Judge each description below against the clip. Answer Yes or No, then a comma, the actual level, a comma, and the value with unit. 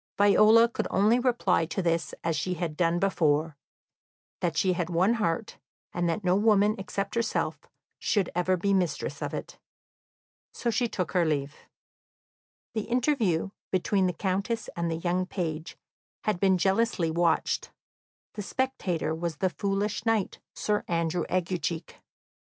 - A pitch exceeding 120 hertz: Yes, medium, 185 Hz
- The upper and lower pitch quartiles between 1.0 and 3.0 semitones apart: No, average, 3.7 semitones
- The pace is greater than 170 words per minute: No, average, 145 wpm